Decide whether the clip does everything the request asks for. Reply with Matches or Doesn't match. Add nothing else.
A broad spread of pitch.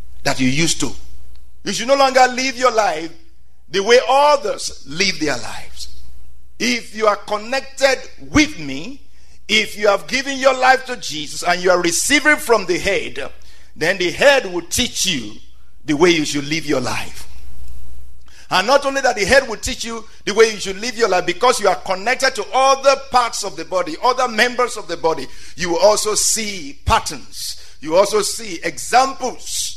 Matches